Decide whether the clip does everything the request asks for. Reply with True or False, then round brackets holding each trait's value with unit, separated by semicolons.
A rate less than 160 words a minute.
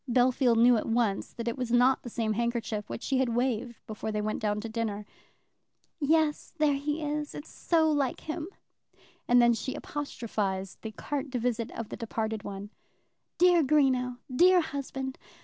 False (175 wpm)